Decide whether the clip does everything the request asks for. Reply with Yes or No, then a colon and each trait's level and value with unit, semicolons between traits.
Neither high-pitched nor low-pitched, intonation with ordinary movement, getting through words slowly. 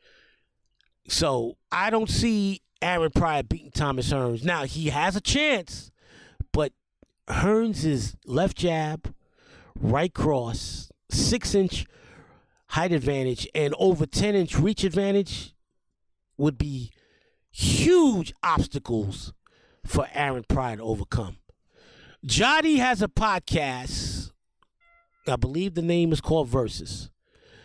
No: medium, 160 Hz; wide, 7.5 semitones; slow, 110 wpm